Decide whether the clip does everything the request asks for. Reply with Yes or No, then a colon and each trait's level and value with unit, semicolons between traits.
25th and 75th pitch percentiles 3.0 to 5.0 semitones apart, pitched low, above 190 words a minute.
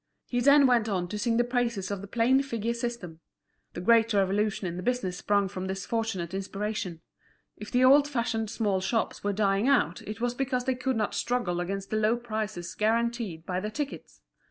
No: average, 3.7 semitones; high, 215 Hz; average, 200 wpm